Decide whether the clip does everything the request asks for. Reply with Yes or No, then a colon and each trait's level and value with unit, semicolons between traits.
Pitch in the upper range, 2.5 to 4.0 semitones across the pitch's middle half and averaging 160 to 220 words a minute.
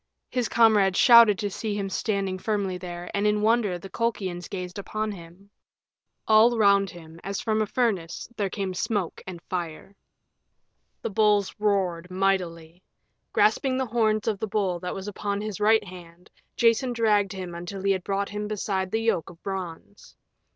Yes: high, 200 Hz; average, 2.8 semitones; average, 170 wpm